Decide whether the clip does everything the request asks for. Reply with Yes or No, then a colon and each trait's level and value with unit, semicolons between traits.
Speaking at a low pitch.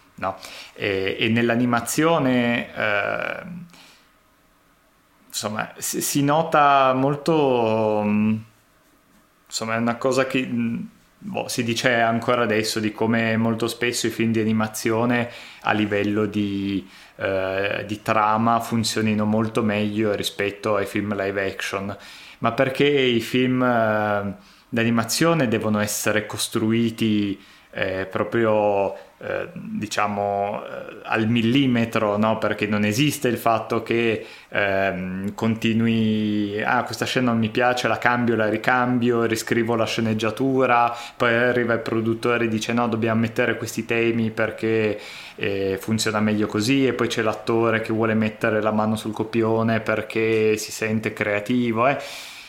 Yes: low, 115 Hz